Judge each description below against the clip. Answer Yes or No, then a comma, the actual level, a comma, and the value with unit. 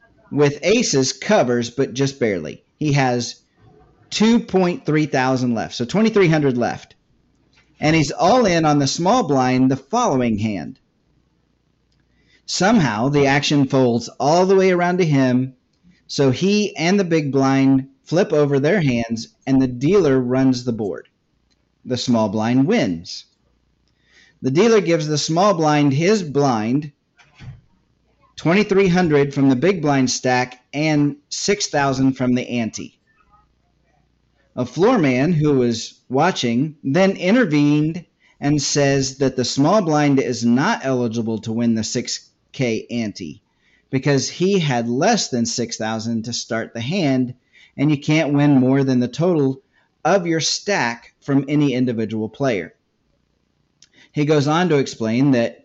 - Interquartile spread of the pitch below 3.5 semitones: No, average, 3.8 semitones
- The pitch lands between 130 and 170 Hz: Yes, medium, 140 Hz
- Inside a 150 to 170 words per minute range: No, slow, 135 wpm